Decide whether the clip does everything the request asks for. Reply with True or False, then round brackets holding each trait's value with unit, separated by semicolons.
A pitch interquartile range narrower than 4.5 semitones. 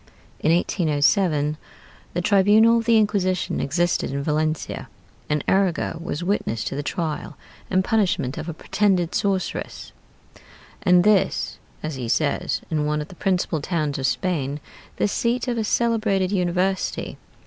False (4.8 semitones)